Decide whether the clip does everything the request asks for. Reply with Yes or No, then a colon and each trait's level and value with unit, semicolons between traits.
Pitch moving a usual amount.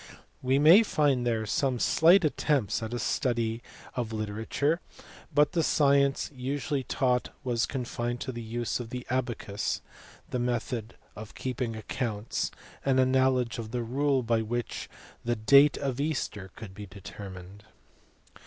Yes: average, 3.4 semitones